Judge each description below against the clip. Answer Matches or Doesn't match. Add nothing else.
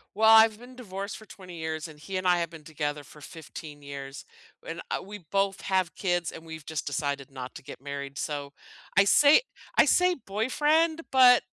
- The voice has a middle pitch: Matches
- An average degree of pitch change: Doesn't match